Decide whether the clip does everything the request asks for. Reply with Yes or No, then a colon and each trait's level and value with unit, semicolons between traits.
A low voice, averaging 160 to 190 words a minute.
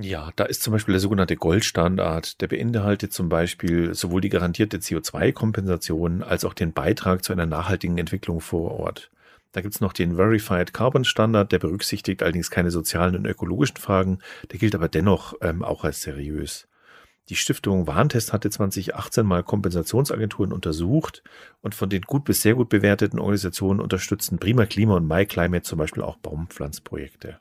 Yes: very low, 95 Hz; average, 165 wpm